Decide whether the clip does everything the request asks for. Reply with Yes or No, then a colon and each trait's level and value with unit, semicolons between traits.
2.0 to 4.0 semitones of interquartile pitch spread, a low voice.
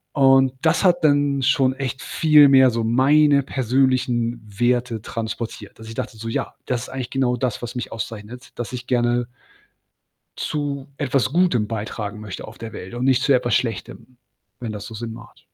Yes: average, 2.8 semitones; low, 125 Hz